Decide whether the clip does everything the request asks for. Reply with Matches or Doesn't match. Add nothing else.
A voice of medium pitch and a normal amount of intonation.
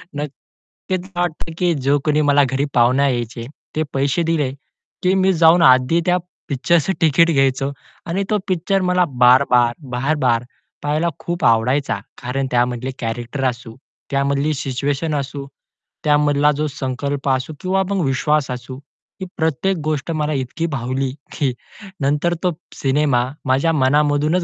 Matches